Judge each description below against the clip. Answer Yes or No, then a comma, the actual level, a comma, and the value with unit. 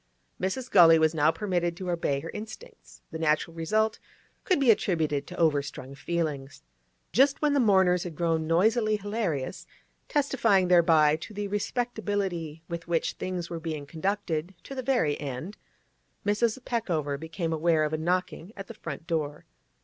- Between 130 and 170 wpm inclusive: Yes, average, 155 wpm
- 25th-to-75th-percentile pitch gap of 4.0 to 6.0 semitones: Yes, average, 4.6 semitones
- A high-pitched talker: No, medium, 175 Hz